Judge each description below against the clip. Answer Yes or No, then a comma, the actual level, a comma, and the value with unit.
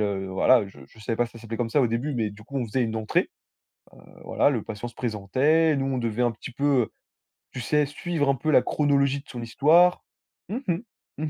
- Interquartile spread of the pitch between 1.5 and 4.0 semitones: No, average, 4.4 semitones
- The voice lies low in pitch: Yes, low, 120 Hz